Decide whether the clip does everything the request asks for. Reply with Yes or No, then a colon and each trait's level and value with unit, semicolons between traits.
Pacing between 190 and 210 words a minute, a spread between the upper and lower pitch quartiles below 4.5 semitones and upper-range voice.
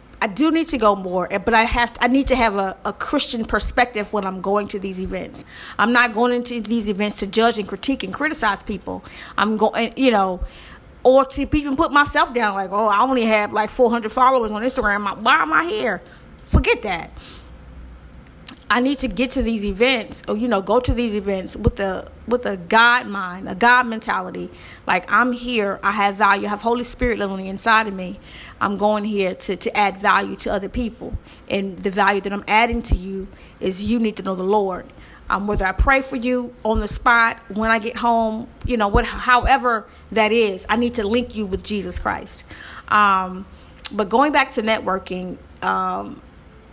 Yes: fast, 205 wpm; average, 3.7 semitones; high, 215 Hz